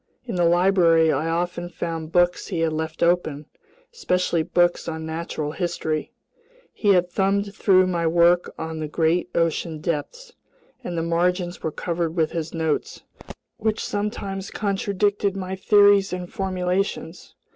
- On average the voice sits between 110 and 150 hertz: No, medium, 175 Hz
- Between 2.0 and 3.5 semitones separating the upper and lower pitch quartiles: Yes, average, 2.8 semitones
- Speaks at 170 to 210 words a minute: No, average, 145 wpm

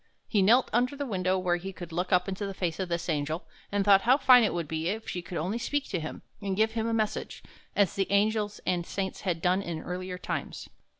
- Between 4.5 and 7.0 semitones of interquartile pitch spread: No, average, 3.4 semitones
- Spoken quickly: Yes, fast, 245 wpm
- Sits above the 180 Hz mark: Yes, high, 190 Hz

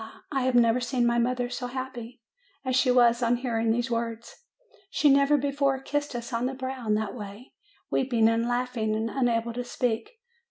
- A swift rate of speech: No, average, 190 wpm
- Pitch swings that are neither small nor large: No, narrow, 2.1 semitones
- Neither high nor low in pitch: No, high, 245 Hz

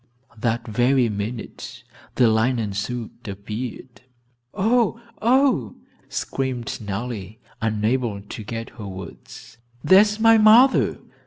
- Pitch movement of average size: Yes, average, 4.2 semitones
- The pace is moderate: No, slow, 105 wpm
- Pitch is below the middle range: Yes, low, 120 Hz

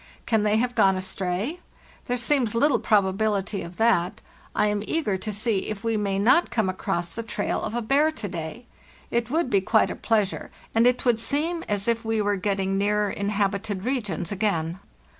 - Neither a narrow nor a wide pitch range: Yes, average, 3.2 semitones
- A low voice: No, high, 210 Hz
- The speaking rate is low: No, average, 190 wpm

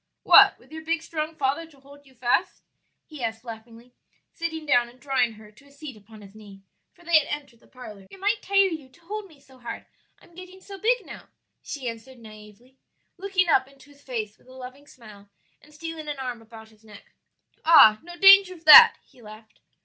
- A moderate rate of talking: No, fast, 210 wpm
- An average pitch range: No, wide, 6.3 semitones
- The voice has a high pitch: Yes, very high, 270 Hz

